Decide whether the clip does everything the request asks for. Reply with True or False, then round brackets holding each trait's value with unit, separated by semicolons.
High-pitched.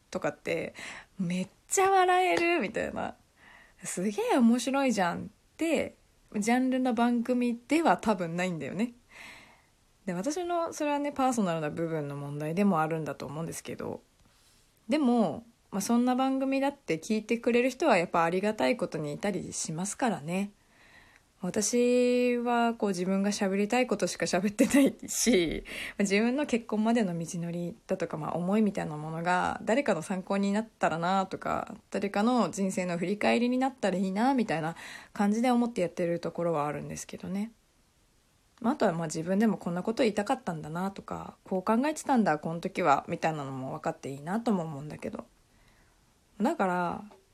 True (205 Hz)